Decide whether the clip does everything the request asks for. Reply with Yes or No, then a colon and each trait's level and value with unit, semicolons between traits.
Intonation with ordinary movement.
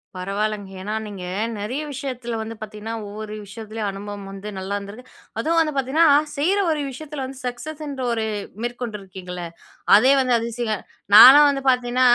Yes: average, 4.4 semitones